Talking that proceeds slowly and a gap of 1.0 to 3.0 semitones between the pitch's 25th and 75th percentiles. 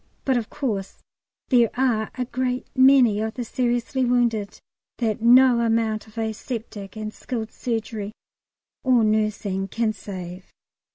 Yes: slow, 130 wpm; narrow, 2.5 semitones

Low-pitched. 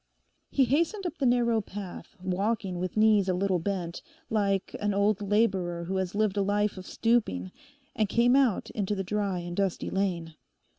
No: high, 200 Hz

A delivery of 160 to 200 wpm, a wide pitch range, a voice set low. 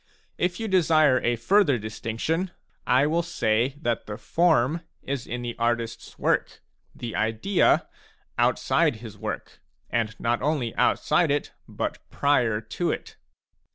No: average, 150 wpm; wide, 5.9 semitones; low, 125 Hz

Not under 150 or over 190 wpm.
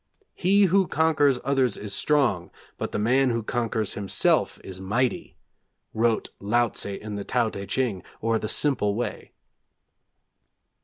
No: average, 140 wpm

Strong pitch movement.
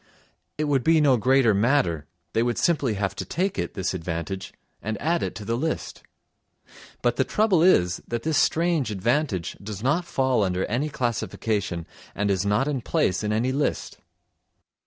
Yes: wide, 6.4 semitones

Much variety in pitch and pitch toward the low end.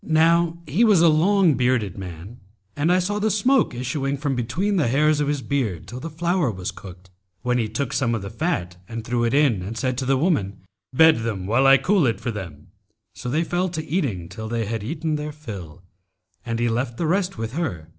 Yes: wide, 6.4 semitones; low, 130 Hz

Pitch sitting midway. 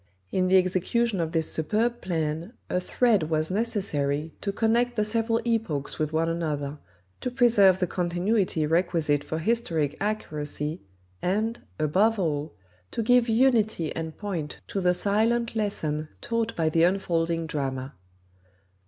Yes: medium, 180 Hz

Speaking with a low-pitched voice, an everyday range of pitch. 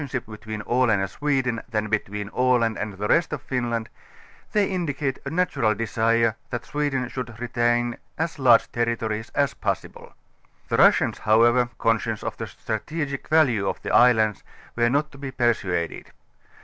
Yes: low, 120 Hz; average, 3.5 semitones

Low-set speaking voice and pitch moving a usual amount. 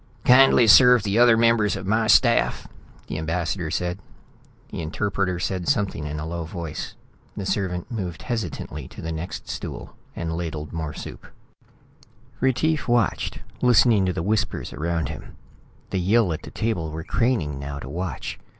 No: very low, 90 Hz; wide, 5.7 semitones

